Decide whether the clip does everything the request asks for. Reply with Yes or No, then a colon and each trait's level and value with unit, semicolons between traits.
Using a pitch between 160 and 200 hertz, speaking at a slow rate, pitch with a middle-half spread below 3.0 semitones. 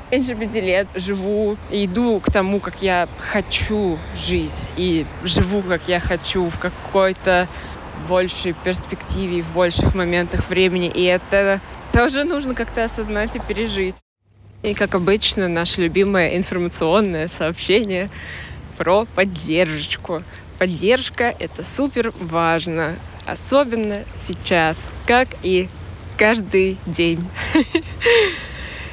No: high, 190 Hz; slow, 105 wpm; average, 3.3 semitones